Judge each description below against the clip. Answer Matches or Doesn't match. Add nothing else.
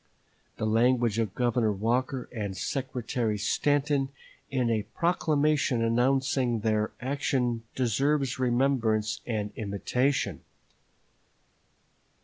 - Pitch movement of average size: Matches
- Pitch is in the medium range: Doesn't match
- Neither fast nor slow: Doesn't match